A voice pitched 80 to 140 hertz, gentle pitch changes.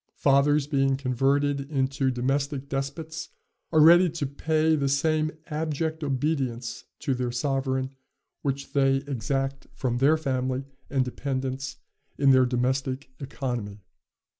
Yes: low, 135 Hz; narrow, 1.8 semitones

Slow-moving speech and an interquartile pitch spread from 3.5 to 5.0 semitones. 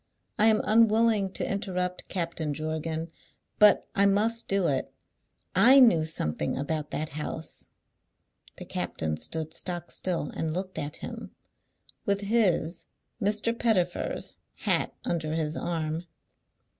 Yes: slow, 125 wpm; average, 4.7 semitones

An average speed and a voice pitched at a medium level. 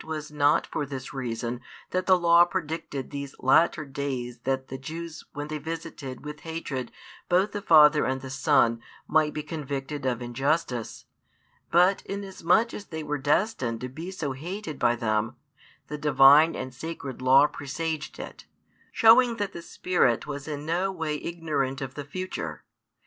Yes: average, 160 wpm; medium, 150 Hz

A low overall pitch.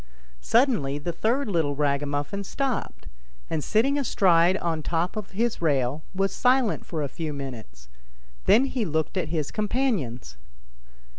No: medium, 170 Hz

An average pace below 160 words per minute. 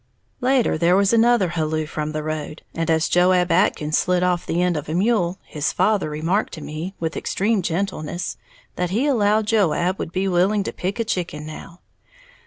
No: average, 190 wpm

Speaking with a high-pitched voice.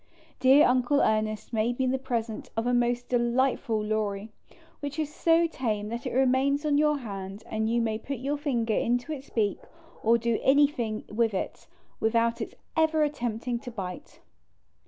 Yes: high, 240 Hz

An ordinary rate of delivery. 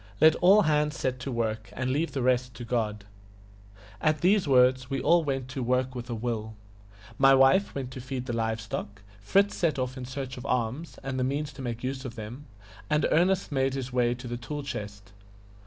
No: fast, 210 wpm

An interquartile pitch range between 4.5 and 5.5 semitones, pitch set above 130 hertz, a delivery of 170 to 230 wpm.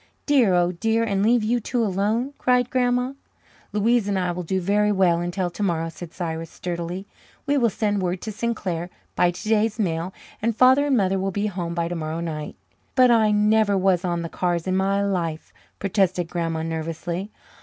No: average, 4.1 semitones; high, 190 Hz; average, 185 wpm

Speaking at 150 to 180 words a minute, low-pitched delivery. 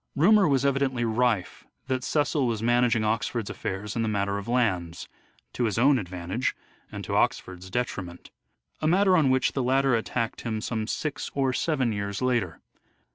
Yes: average, 170 wpm; low, 120 Hz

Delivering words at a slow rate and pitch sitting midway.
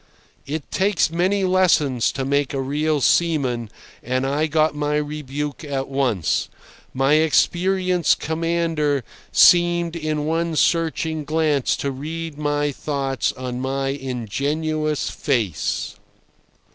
Yes: slow, 115 wpm; medium, 150 Hz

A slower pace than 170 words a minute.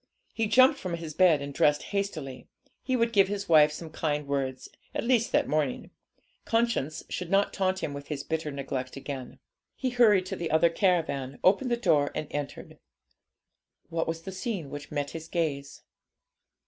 No: average, 175 wpm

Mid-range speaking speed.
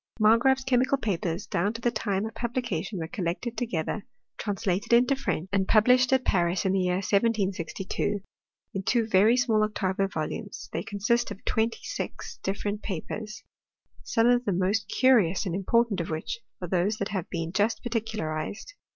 Yes: average, 165 wpm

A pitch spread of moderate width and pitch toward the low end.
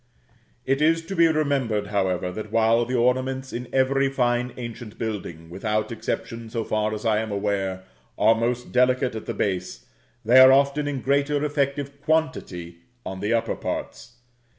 Yes: average, 4.3 semitones; low, 120 Hz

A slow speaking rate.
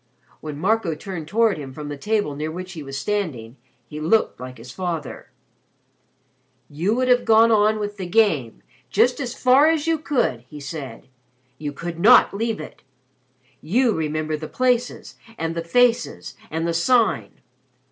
No: average, 165 wpm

